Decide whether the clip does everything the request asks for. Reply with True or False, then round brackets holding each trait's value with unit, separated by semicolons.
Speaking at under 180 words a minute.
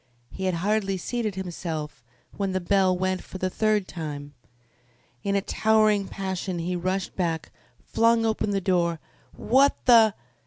True (150 wpm)